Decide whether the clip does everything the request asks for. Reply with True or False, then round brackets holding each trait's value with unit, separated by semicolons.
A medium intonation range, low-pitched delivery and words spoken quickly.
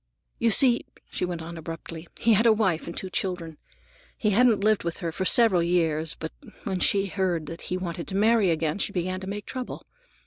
False (3.7 semitones; 185 Hz; 210 wpm)